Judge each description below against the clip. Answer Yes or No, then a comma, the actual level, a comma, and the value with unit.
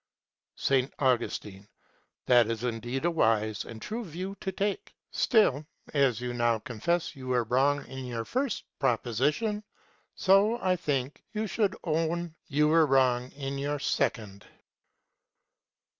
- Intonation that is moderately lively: No, wide, 6.1 semitones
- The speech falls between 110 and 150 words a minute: Yes, slow, 135 wpm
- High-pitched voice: No, low, 135 Hz